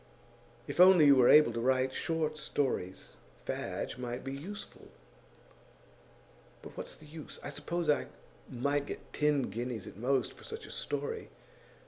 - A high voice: No, medium, 140 Hz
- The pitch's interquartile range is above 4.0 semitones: No, average, 3.6 semitones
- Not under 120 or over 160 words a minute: Yes, average, 150 wpm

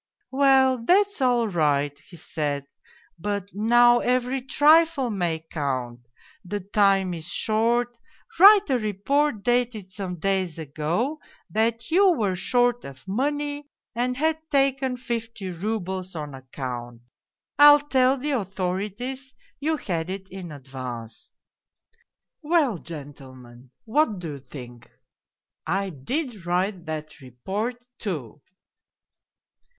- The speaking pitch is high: Yes, high, 205 Hz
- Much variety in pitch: Yes, wide, 8.3 semitones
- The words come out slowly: Yes, slow, 125 wpm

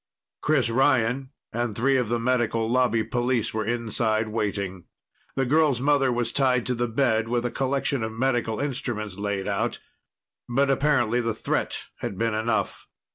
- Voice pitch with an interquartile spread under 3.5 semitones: Yes, average, 2.9 semitones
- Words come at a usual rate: Yes, average, 160 wpm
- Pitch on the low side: Yes, low, 120 Hz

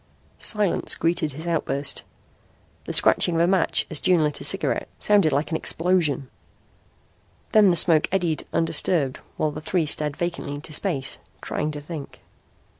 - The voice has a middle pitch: Yes, medium, 160 Hz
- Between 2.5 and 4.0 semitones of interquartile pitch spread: Yes, average, 2.9 semitones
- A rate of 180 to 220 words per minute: No, average, 155 wpm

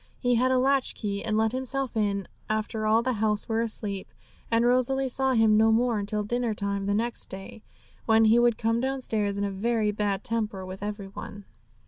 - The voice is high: Yes, high, 220 Hz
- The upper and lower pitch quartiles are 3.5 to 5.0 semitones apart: No, average, 2.7 semitones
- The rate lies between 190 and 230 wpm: Yes, fast, 205 wpm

